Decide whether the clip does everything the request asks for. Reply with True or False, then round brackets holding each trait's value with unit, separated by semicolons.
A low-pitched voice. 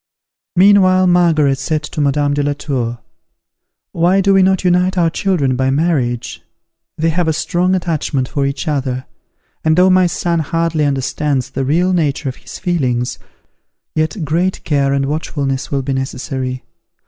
False (150 Hz)